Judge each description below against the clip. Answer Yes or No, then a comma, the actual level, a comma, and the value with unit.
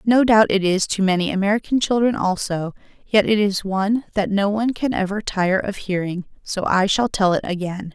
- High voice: Yes, high, 200 Hz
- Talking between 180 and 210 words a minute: Yes, fast, 205 wpm